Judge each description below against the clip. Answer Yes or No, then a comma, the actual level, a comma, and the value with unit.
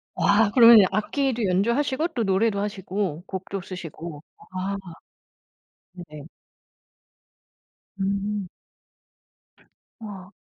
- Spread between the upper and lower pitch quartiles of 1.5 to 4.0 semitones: Yes, average, 3.2 semitones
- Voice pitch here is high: Yes, high, 200 Hz